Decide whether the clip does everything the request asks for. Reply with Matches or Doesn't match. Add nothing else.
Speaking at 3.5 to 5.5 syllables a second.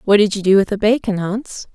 Doesn't match